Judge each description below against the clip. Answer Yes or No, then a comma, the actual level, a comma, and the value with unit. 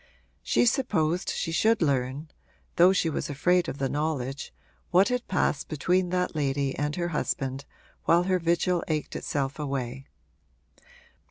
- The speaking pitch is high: No, medium, 155 Hz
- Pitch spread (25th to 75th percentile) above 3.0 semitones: Yes, average, 4.4 semitones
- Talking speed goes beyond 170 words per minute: No, average, 145 wpm